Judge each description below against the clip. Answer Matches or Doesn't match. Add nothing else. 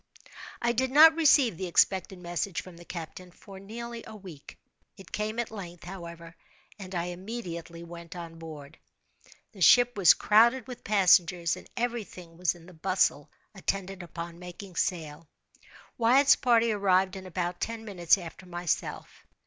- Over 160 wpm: Doesn't match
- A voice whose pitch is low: Doesn't match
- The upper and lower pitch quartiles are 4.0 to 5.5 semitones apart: Matches